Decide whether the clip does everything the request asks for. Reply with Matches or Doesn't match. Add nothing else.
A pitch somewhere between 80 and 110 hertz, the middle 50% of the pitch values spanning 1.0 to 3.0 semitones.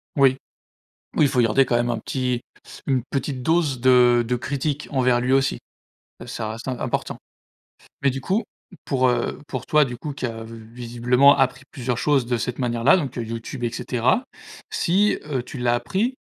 Doesn't match